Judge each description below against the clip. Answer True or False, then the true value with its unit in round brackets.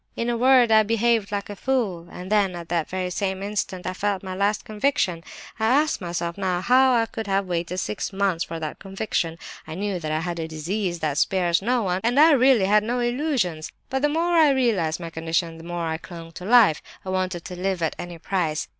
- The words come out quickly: True (225 wpm)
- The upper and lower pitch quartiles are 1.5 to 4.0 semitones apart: False (4.9 semitones)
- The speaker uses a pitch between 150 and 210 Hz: True (190 Hz)